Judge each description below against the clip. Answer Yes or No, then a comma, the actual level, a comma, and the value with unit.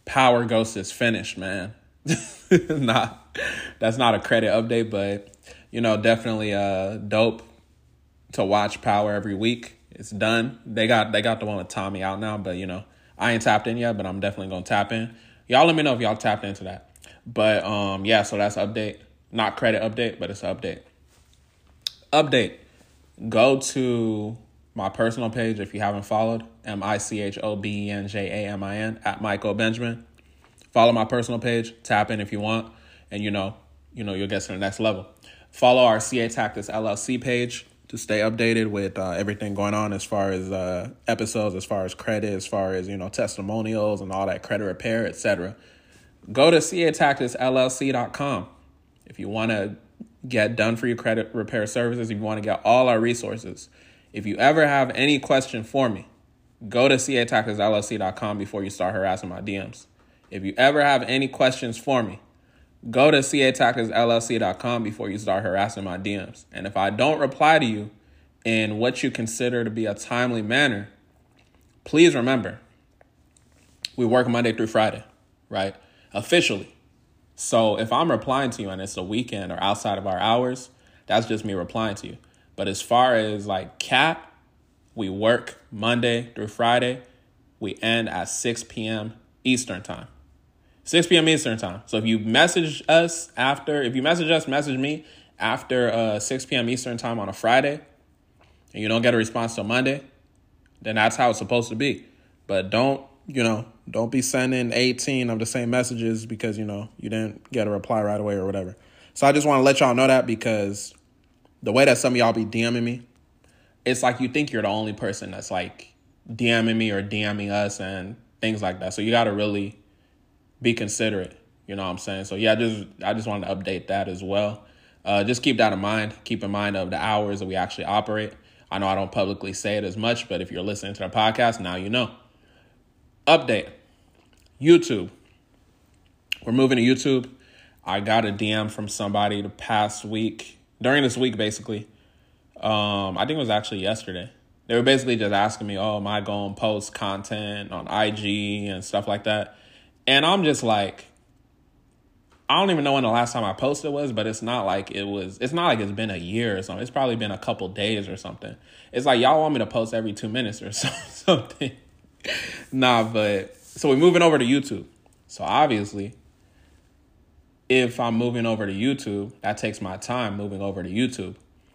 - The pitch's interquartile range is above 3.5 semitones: No, average, 3.2 semitones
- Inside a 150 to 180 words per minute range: No, average, 190 wpm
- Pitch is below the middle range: Yes, low, 110 Hz